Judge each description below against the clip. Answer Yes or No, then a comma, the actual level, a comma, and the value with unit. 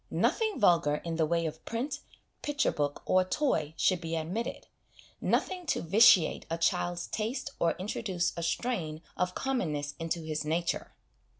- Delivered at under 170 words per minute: Yes, average, 155 wpm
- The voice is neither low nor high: Yes, medium, 175 Hz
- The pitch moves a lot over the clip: Yes, wide, 6.1 semitones